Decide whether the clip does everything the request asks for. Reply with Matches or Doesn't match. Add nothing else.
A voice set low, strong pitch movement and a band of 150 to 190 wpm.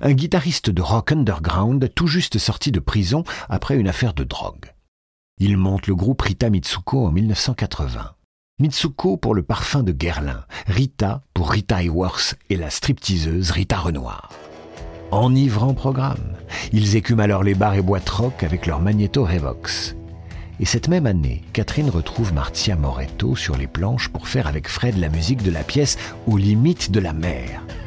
Matches